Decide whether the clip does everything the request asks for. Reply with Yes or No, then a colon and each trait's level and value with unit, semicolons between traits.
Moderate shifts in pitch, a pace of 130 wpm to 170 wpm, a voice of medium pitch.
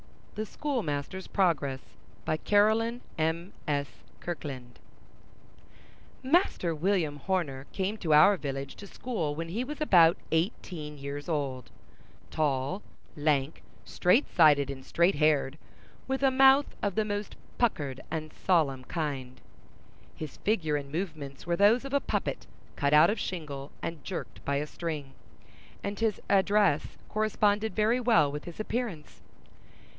No: wide, 6.2 semitones; slow, 135 wpm; medium, 165 Hz